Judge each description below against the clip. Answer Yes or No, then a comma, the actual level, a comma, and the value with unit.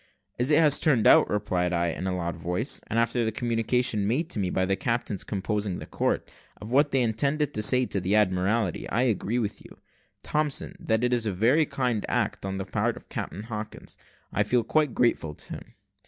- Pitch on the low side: Yes, low, 110 Hz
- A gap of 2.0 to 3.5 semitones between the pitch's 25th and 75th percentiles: No, average, 4.3 semitones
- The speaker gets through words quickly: Yes, fast, 215 wpm